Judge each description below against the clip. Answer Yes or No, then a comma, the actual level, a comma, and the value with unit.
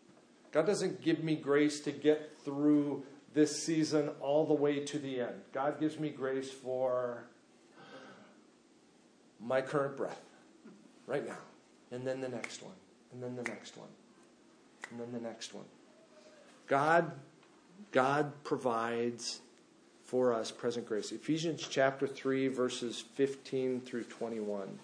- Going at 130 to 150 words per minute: Yes, slow, 135 wpm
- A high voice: No, low, 135 Hz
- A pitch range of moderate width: Yes, average, 3.6 semitones